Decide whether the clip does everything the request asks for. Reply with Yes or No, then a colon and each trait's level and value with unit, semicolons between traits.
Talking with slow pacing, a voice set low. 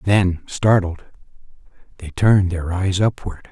Yes: slow, 120 wpm; very low, 95 Hz